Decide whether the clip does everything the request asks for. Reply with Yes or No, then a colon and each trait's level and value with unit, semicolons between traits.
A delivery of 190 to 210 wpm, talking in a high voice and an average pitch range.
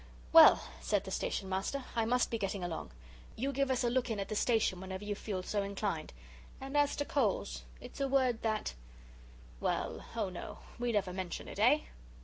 Yes: average, 195 wpm; high, 215 Hz; average, 5.0 semitones